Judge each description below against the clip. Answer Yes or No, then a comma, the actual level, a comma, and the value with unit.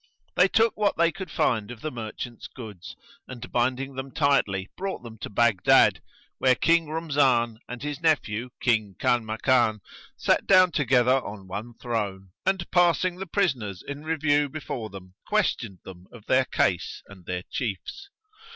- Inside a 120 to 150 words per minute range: No, average, 160 wpm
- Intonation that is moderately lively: No, wide, 6.3 semitones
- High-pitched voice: No, low, 125 Hz